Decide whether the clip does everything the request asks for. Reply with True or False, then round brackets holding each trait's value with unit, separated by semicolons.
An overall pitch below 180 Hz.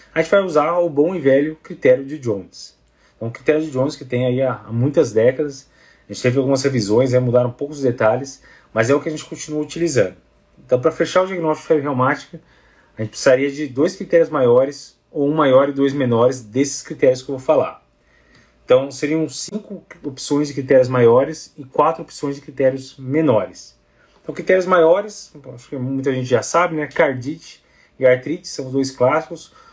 True (140 Hz)